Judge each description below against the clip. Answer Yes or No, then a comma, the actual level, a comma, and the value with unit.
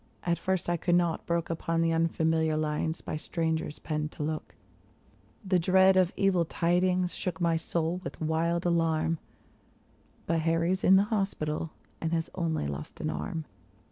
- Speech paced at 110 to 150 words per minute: No, average, 165 wpm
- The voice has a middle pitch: Yes, medium, 165 Hz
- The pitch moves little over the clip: Yes, narrow, 1.7 semitones